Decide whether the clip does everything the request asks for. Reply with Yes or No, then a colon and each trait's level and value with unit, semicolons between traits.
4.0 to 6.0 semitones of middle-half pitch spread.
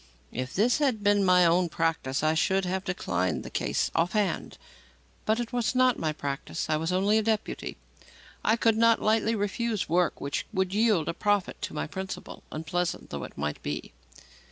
Yes: average, 5.1 semitones